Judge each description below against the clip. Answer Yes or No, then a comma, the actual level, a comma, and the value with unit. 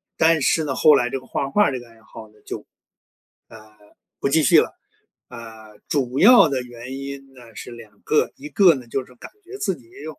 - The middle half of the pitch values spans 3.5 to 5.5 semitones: Yes, average, 4.3 semitones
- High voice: No, low, 130 Hz